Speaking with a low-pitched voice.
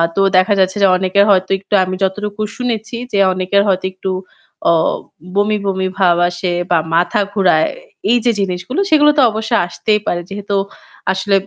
No: high, 195 Hz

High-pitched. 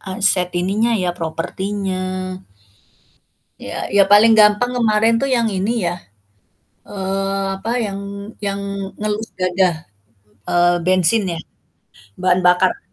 Yes: high, 195 Hz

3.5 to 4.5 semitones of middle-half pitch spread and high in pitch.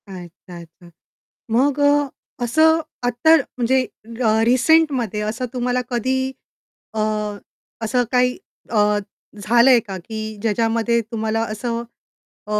No: average, 2.8 semitones; high, 235 Hz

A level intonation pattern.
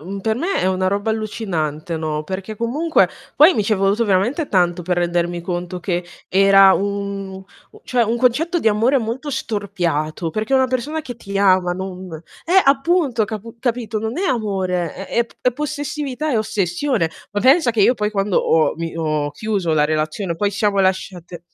No: average, 4.9 semitones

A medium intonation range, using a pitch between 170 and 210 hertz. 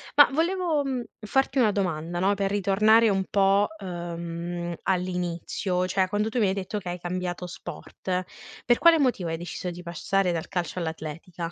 Yes: average, 3.2 semitones; medium, 185 Hz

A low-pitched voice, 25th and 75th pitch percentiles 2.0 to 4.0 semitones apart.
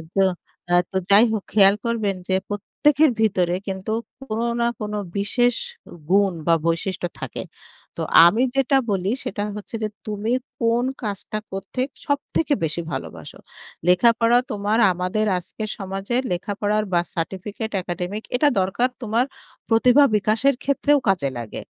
No: high, 210 Hz; average, 3.6 semitones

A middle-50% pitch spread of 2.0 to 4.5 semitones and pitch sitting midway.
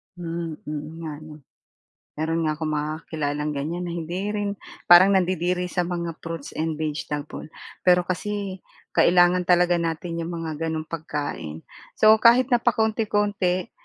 Yes: average, 2.7 semitones; medium, 170 Hz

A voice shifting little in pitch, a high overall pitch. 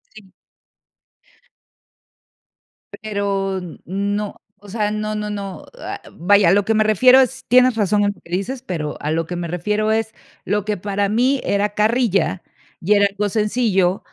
Yes: narrow, 1.9 semitones; high, 205 Hz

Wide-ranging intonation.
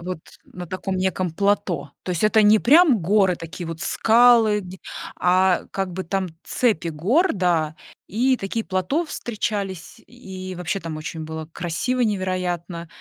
No: average, 3.8 semitones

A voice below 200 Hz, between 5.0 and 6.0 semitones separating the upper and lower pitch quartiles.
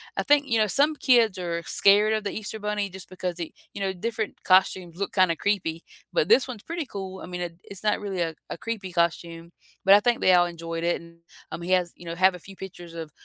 No: medium, 185 Hz; average, 3.4 semitones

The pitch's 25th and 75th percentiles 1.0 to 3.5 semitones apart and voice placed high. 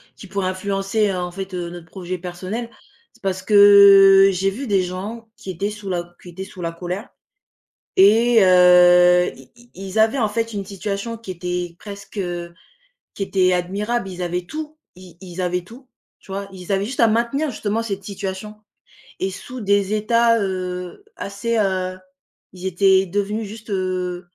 Yes: average, 2.7 semitones; high, 195 Hz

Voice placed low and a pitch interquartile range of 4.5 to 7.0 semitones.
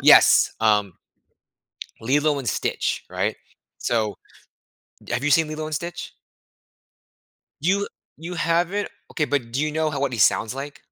No: medium, 145 Hz; average, 4.8 semitones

